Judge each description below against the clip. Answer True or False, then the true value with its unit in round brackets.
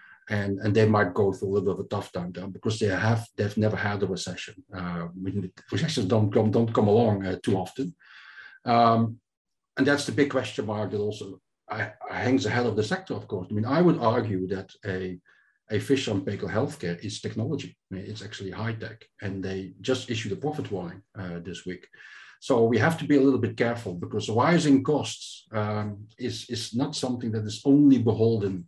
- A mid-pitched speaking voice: False (105 Hz)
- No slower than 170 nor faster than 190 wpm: False (205 wpm)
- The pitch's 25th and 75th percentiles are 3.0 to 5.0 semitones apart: True (3.8 semitones)